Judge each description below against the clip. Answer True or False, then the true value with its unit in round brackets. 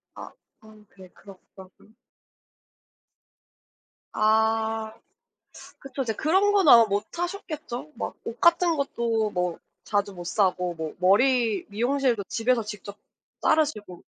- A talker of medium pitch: False (220 Hz)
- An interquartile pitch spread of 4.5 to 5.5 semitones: True (5.2 semitones)